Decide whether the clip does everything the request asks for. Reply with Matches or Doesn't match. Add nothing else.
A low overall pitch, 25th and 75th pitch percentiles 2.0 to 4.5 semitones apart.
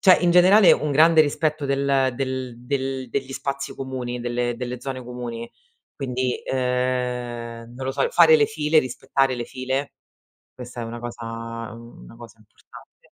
Matches